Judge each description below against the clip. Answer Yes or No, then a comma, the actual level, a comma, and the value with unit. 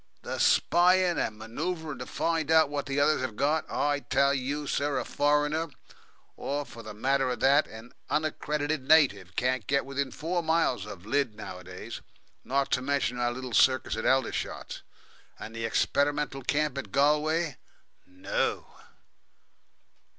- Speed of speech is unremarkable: Yes, average, 150 wpm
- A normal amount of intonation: Yes, average, 3.4 semitones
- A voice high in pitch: No, medium, 140 Hz